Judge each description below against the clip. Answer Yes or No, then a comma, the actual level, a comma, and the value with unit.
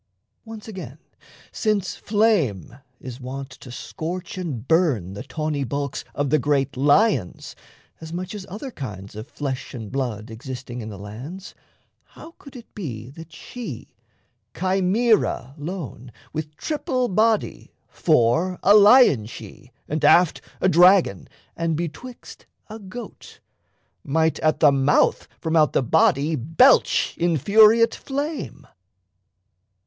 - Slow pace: Yes, slow, 130 wpm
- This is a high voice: No, medium, 160 Hz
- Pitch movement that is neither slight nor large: No, wide, 7.4 semitones